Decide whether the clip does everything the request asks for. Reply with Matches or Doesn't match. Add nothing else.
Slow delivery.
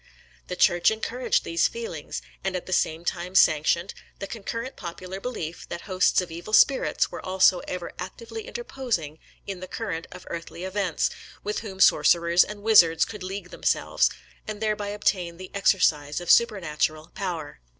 Doesn't match